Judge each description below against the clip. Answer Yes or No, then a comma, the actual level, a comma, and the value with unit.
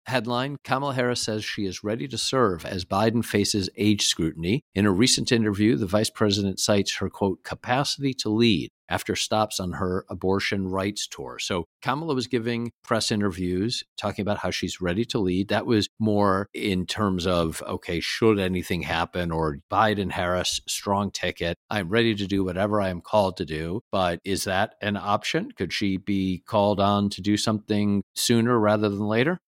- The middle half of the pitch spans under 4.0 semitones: Yes, average, 2.9 semitones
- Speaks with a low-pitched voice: Yes, low, 105 Hz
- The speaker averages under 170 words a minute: No, average, 180 wpm